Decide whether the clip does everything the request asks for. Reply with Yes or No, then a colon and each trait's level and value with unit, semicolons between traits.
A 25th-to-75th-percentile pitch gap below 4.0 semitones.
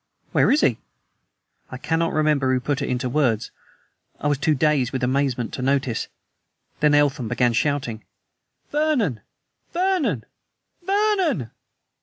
No: average, 4.4 semitones